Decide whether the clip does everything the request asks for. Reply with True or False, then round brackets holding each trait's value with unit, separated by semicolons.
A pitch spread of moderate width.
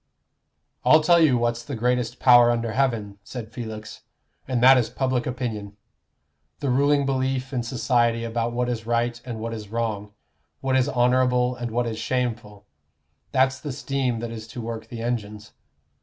False (2.1 semitones)